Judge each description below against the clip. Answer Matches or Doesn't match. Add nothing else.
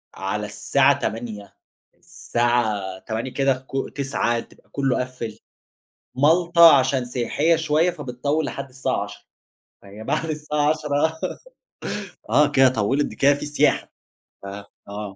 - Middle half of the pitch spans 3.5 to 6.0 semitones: Matches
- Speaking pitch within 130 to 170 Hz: Matches